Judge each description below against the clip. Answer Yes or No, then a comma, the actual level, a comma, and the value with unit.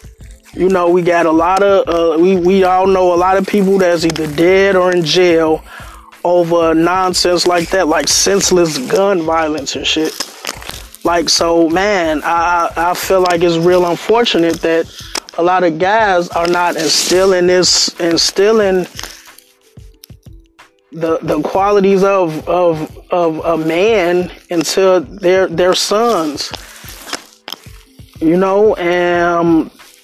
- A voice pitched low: No, medium, 175 Hz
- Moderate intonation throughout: No, narrow, 2.0 semitones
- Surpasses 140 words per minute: No, slow, 135 wpm